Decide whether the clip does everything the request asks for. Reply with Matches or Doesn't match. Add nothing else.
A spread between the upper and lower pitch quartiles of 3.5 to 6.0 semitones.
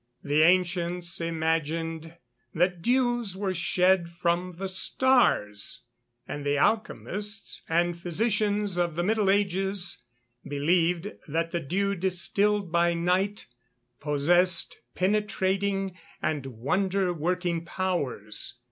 Doesn't match